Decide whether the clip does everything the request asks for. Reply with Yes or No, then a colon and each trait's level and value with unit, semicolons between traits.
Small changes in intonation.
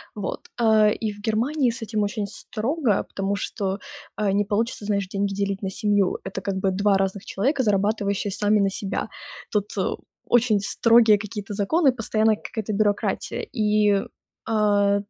Yes: narrow, 1.6 semitones